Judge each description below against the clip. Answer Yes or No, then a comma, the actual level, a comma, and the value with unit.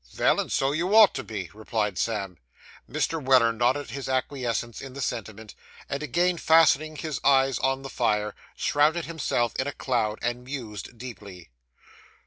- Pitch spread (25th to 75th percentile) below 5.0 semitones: Yes, average, 4.5 semitones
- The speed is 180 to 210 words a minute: No, average, 160 wpm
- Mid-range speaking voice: No, low, 130 Hz